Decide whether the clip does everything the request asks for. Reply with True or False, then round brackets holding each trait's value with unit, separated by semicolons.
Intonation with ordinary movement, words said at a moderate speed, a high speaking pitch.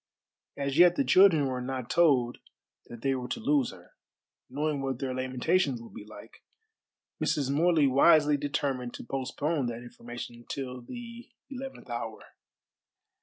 False (3.7 semitones; 145 wpm; 135 Hz)